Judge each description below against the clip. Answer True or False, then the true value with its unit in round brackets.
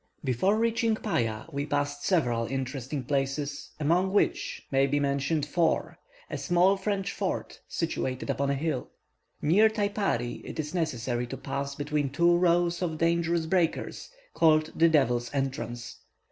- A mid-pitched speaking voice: True (150 Hz)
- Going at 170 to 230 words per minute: False (145 wpm)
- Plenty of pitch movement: False (4.3 semitones)